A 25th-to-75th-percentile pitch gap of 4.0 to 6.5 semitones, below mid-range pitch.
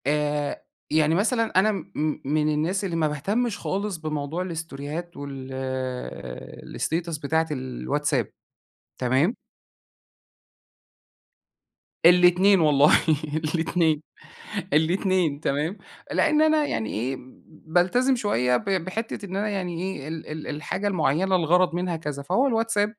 No: average, 4.6 semitones; medium, 165 Hz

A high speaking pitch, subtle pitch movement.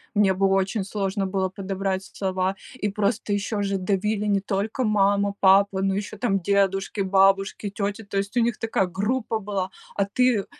Yes: high, 200 Hz; narrow, 1.3 semitones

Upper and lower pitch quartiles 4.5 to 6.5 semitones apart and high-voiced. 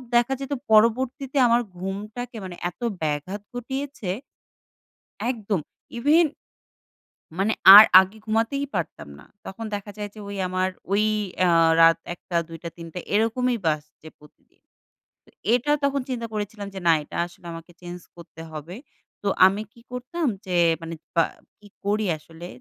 Yes: wide, 5.6 semitones; high, 205 Hz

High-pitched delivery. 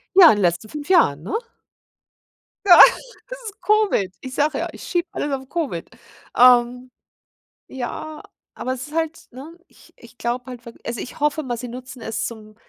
Yes: very high, 255 Hz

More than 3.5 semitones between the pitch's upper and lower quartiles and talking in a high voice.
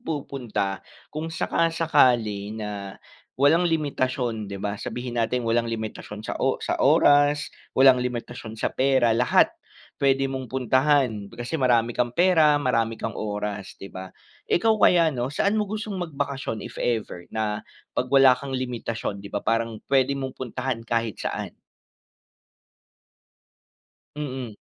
No: average, 3.9 semitones; low, 125 Hz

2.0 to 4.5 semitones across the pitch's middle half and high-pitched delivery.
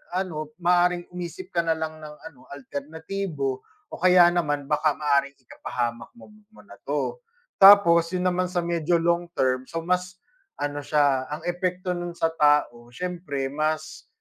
No: average, 3.5 semitones; medium, 165 Hz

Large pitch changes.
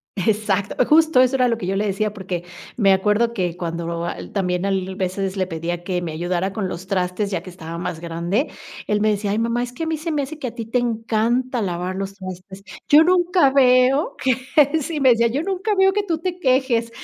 Yes: wide, 5.7 semitones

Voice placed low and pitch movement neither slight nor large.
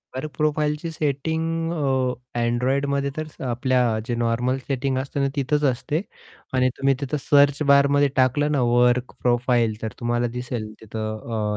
Yes: low, 130 Hz; average, 3.0 semitones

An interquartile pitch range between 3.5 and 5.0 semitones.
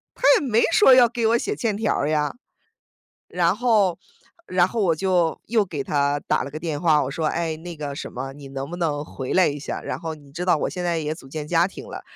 Yes: average, 4.4 semitones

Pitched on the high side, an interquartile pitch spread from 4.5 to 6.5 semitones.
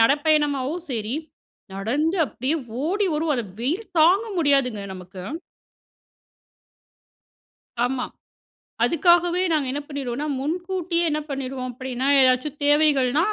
No: very high, 285 Hz; average, 4.1 semitones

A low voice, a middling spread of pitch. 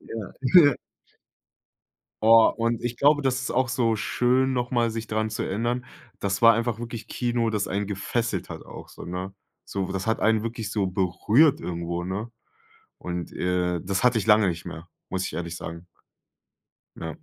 Yes: low, 110 Hz; average, 4.3 semitones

